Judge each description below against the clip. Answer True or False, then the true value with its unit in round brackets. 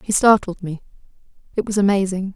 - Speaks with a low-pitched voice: False (195 Hz)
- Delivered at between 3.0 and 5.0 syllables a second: False (5.9 syllables/s)